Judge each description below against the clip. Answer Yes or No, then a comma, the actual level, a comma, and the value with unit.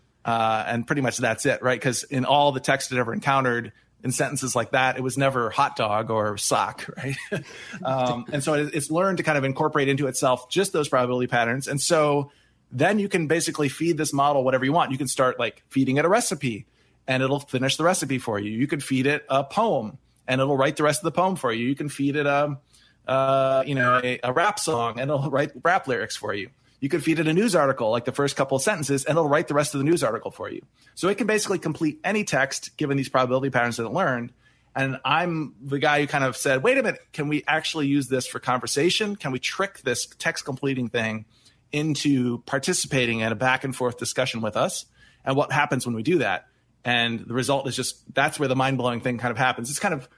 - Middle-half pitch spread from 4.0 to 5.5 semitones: No, average, 3.1 semitones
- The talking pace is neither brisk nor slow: No, fast, 240 wpm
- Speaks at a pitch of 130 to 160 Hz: Yes, low, 135 Hz